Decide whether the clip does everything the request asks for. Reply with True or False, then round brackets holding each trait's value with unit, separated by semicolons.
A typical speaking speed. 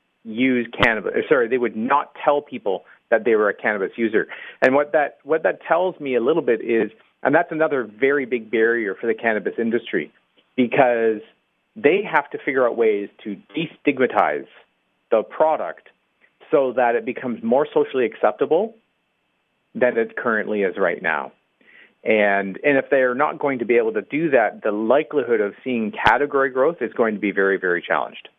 True (180 wpm)